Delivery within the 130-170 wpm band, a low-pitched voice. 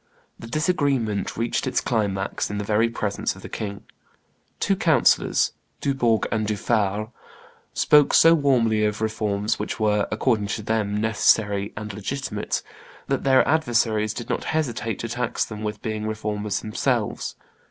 Yes: average, 145 wpm; low, 110 Hz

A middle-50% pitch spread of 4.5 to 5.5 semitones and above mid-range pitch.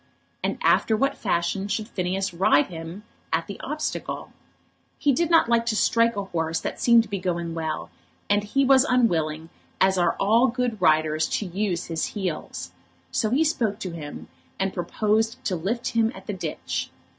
Yes: average, 5.2 semitones; high, 200 Hz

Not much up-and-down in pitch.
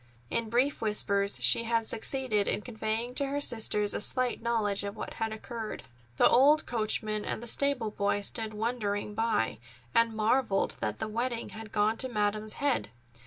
Yes: narrow, 2.3 semitones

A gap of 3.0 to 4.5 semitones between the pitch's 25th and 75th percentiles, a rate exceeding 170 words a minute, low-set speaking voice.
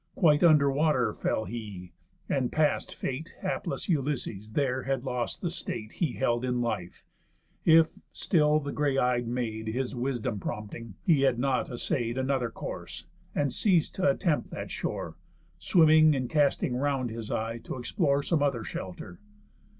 No: average, 4.1 semitones; average, 155 wpm; low, 130 Hz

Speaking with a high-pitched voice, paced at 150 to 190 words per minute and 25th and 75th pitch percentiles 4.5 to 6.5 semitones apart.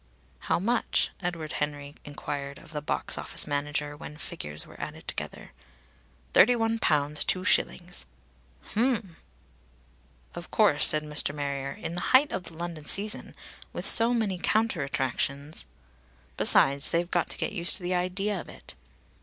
No: medium, 165 Hz; average, 155 wpm; average, 5.1 semitones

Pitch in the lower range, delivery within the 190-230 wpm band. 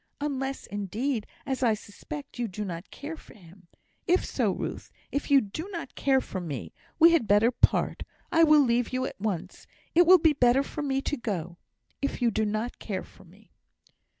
No: high, 245 Hz; average, 195 wpm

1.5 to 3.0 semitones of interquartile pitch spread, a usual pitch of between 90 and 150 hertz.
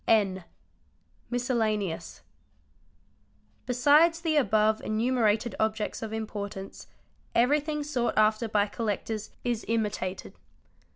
No: average, 2.7 semitones; high, 220 Hz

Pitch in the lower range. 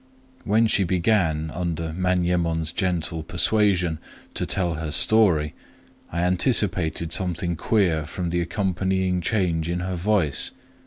Yes: very low, 90 Hz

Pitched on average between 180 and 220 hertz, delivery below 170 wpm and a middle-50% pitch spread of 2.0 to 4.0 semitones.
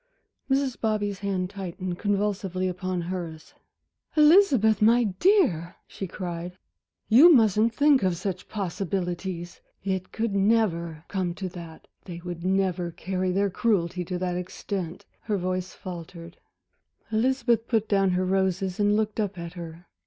Yes: high, 190 Hz; average, 140 wpm; average, 3.1 semitones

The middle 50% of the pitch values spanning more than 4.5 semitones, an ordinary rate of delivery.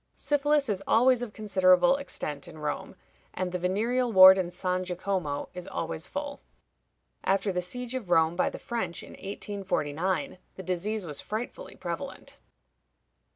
Yes: average, 4.9 semitones; average, 150 wpm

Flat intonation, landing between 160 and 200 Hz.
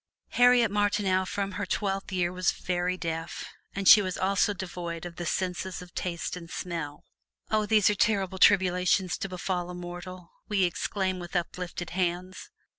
Yes: narrow, 1.8 semitones; medium, 185 Hz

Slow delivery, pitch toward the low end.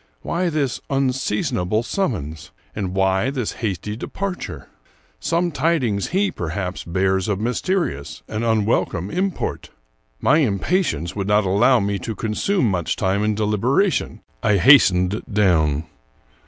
Yes: slow, 125 wpm; low, 105 Hz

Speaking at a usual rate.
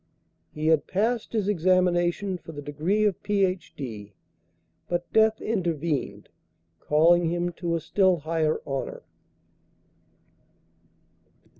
No: slow, 105 wpm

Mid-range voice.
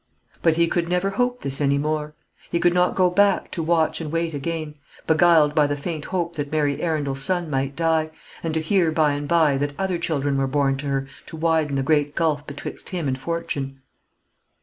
Yes: medium, 155 Hz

